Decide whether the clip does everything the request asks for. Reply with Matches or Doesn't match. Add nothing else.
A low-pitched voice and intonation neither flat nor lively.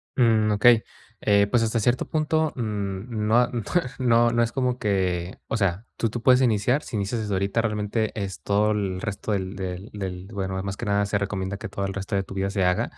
Matches